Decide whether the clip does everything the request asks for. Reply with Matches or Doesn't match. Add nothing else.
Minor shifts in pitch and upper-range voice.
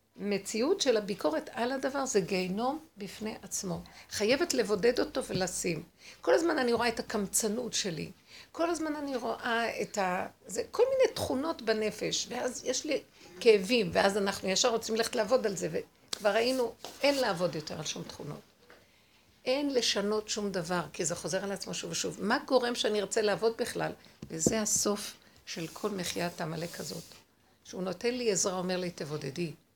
Doesn't match